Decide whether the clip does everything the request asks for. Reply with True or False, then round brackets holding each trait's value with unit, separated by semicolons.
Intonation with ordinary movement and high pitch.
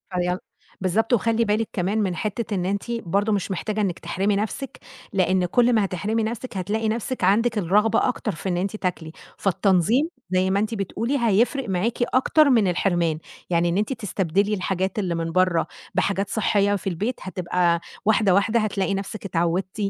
True (3.3 semitones; 200 Hz)